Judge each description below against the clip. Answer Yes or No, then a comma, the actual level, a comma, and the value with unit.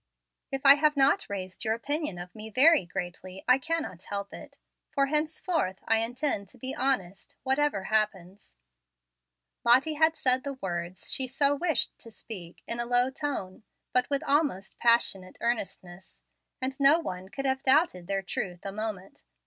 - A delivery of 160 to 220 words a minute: Yes, average, 165 wpm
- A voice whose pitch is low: No, high, 240 Hz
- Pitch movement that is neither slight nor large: No, wide, 6.5 semitones